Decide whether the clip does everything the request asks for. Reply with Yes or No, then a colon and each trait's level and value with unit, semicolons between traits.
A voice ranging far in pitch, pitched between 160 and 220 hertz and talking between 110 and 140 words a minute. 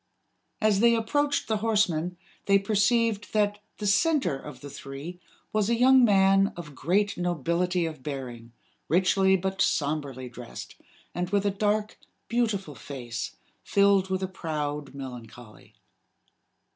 Yes: wide, 5.9 semitones; high, 190 Hz; slow, 135 wpm